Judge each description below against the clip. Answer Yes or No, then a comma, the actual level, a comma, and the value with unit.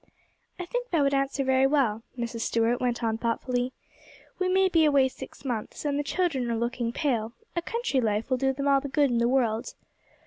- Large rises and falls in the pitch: No, average, 3.5 semitones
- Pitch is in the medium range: No, very high, 265 Hz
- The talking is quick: Yes, fast, 210 wpm